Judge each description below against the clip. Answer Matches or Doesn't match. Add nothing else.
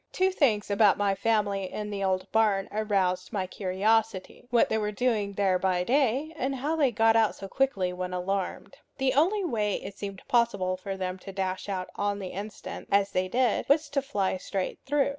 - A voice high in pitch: Matches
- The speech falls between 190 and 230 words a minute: Matches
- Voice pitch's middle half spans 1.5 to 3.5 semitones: Doesn't match